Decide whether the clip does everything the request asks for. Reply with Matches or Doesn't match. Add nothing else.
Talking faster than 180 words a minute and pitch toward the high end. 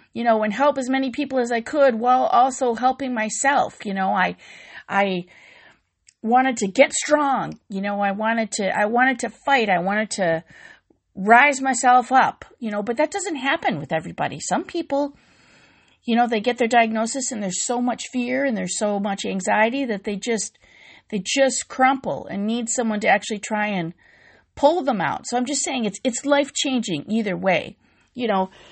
Matches